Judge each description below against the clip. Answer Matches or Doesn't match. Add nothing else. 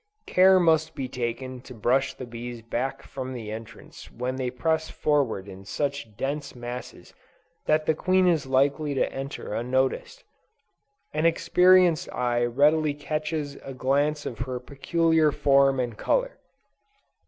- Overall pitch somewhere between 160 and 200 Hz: Doesn't match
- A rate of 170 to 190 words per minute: Doesn't match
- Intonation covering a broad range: Doesn't match